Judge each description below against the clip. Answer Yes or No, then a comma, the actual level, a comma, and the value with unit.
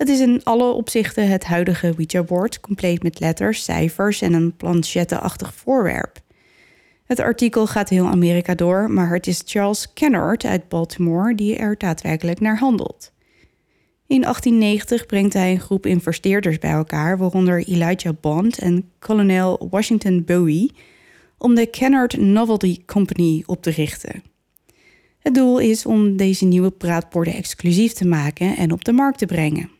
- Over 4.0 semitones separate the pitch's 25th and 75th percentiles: Yes, average, 4.4 semitones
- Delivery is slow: No, average, 150 wpm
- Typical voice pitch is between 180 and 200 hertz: Yes, medium, 185 Hz